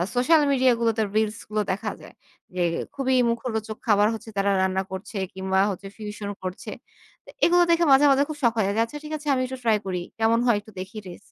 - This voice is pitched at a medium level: No, high, 220 Hz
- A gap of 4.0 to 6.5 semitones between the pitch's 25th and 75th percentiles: Yes, average, 4.3 semitones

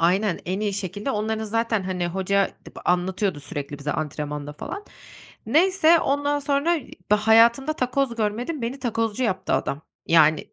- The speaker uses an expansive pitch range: Yes, wide, 6.2 semitones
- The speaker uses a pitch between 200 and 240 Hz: Yes, high, 210 Hz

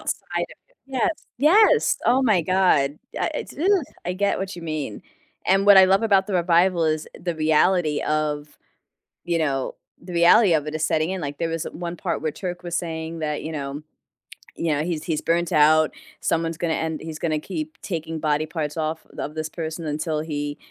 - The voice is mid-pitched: Yes, medium, 165 Hz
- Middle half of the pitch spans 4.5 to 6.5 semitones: No, average, 2.9 semitones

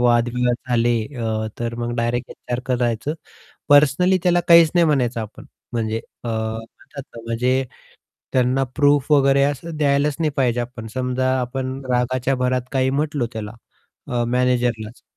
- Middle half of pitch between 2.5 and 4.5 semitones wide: Yes, average, 2.8 semitones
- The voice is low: Yes, low, 125 Hz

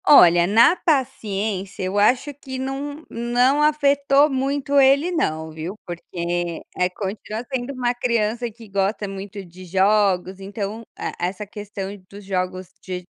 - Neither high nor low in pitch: No, high, 210 Hz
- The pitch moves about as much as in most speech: No, wide, 5.8 semitones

